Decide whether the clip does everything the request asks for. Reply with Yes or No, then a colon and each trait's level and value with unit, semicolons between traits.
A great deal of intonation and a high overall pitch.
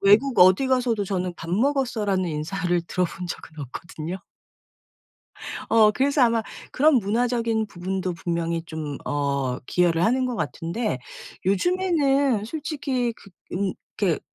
Yes: wide, 6.3 semitones; high, 200 Hz